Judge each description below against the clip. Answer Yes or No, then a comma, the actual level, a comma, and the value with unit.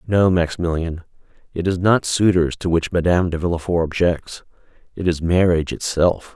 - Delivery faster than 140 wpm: Yes, average, 150 wpm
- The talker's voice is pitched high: No, very low, 85 Hz